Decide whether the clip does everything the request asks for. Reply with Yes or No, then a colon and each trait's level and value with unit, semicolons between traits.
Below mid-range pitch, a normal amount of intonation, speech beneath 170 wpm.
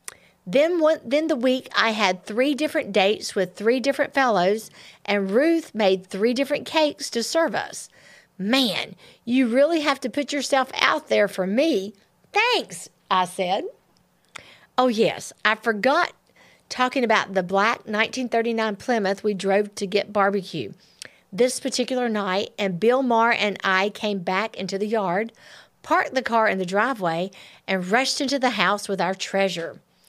No: high, 225 Hz; average, 5.0 semitones; average, 160 wpm